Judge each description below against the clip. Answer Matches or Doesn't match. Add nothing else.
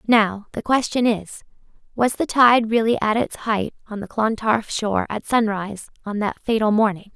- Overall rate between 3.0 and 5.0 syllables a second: Matches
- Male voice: Doesn't match